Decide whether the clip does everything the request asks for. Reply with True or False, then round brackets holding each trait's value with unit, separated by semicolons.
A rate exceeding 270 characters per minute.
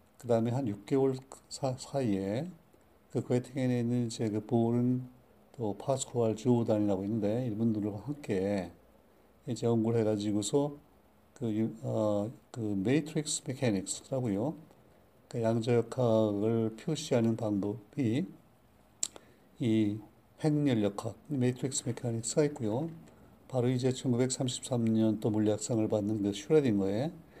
False (255 characters per minute)